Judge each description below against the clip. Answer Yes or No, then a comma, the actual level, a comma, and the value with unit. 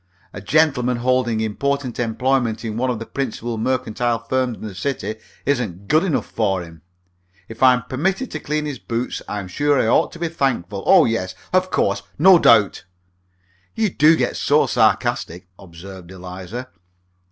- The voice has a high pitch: No, low, 120 Hz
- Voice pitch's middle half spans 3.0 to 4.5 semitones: No, average, 5.2 semitones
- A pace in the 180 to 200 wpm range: No, average, 165 wpm